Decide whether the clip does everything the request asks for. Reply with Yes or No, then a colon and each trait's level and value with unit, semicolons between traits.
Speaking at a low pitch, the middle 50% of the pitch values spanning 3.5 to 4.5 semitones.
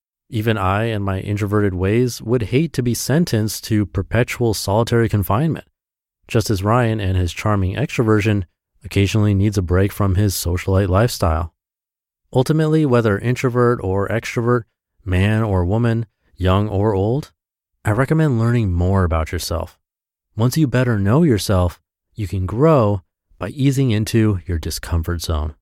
Yes: low, 105 Hz; average, 4.0 semitones